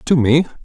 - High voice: No, medium, 145 Hz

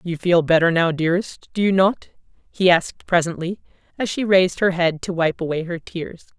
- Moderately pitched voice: Yes, medium, 175 Hz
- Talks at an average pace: Yes, average, 195 wpm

